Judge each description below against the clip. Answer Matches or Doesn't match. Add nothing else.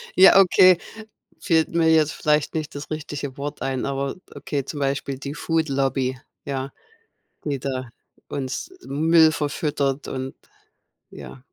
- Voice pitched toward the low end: Doesn't match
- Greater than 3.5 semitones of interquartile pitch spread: Doesn't match